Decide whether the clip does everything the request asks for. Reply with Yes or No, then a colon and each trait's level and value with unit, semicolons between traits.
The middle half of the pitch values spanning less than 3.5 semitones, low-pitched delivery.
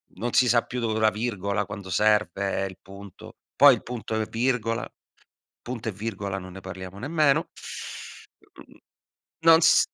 No: average, 3.9 semitones; low, 110 Hz